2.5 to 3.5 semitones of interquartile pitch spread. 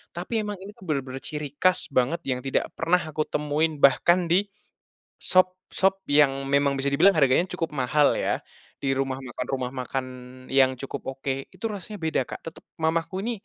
No: average, 5.1 semitones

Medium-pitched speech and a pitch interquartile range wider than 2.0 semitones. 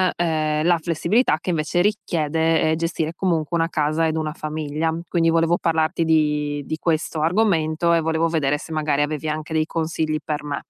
No: medium, 160 Hz; narrow, 1.4 semitones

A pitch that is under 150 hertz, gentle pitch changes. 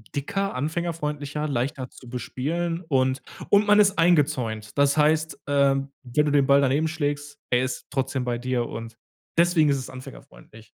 No: medium, 140 Hz; average, 3.6 semitones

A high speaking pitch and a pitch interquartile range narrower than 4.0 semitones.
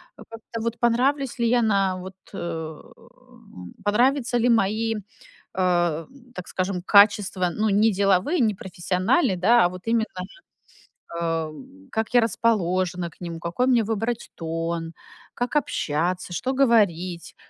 No: high, 200 Hz; average, 4.8 semitones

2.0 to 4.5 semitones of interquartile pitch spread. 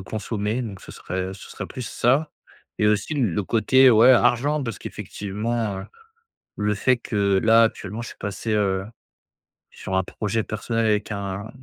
Yes: average, 2.9 semitones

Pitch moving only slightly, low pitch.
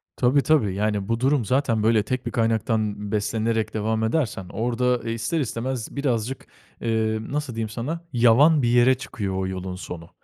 No: average, 3.0 semitones; low, 115 Hz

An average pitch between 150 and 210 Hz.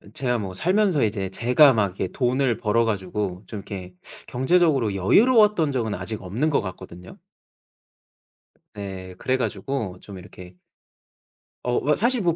No: low, 115 Hz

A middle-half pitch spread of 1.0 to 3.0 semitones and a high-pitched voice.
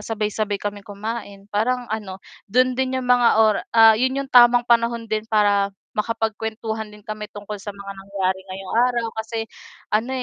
Yes: narrow, 2.4 semitones; high, 220 Hz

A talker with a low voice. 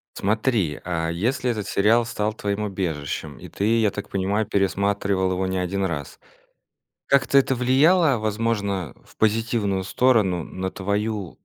Yes: low, 100 Hz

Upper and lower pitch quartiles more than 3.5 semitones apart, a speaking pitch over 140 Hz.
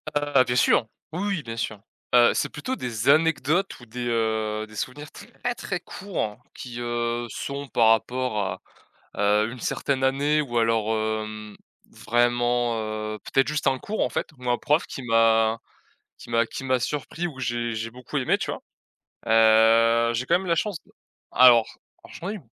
No: average, 3.9 semitones; low, 120 Hz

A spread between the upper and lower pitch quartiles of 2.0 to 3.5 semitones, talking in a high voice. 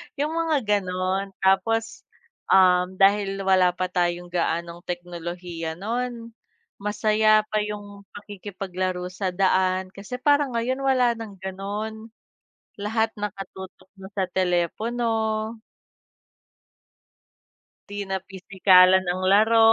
Yes: average, 3.1 semitones; high, 195 Hz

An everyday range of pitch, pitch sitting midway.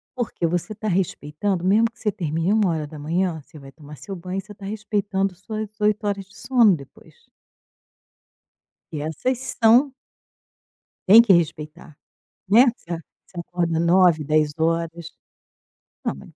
Yes: average, 4.5 semitones; medium, 180 Hz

